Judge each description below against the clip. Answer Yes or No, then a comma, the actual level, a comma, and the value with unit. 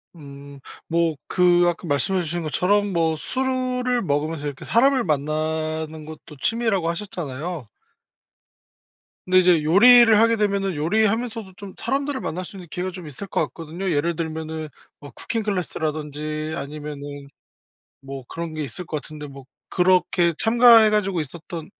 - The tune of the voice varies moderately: Yes, average, 4.8 semitones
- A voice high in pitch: No, medium, 170 Hz